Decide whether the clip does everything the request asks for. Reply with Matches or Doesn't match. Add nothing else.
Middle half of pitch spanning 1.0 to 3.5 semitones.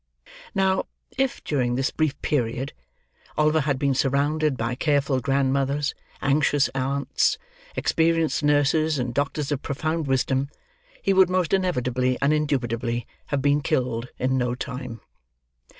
Matches